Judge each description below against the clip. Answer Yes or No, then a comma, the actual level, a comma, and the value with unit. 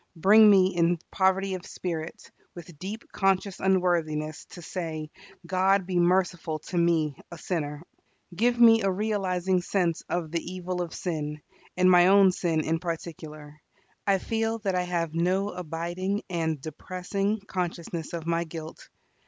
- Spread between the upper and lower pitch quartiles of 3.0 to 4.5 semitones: No, narrow, 2.6 semitones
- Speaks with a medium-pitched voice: Yes, medium, 180 Hz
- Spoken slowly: No, average, 150 wpm